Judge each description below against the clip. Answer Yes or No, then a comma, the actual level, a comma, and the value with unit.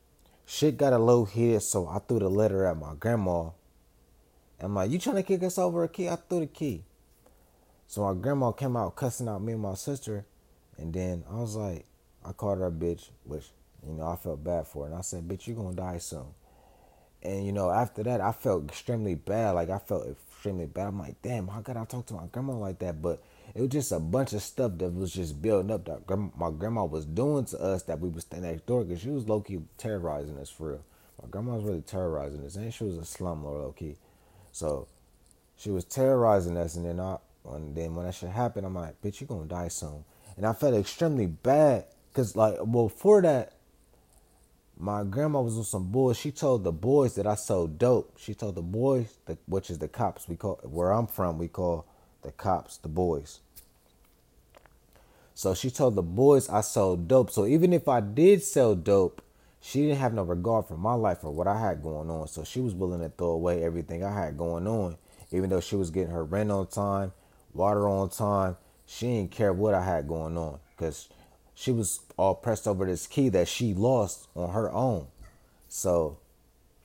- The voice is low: Yes, very low, 95 Hz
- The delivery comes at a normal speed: No, fast, 220 wpm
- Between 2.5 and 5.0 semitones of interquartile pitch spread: No, wide, 5.4 semitones